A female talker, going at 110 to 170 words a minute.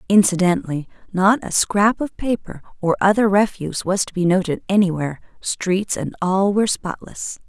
Yes: female; average, 145 wpm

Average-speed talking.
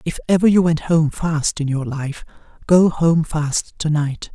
Yes: average, 195 wpm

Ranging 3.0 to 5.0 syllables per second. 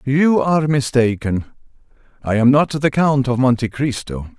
Yes: 4.5 syllables/s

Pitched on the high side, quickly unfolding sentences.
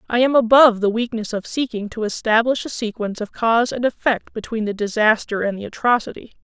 No: high, 225 Hz; average, 195 wpm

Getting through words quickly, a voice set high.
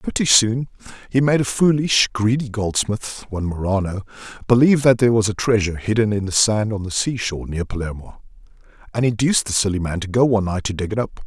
No: fast, 210 wpm; low, 110 Hz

